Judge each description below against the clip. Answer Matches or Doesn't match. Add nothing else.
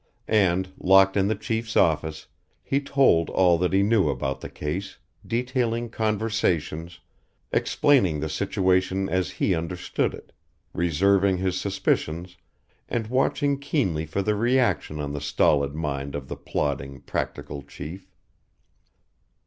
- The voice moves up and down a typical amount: Doesn't match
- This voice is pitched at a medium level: Doesn't match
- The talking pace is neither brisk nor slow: Doesn't match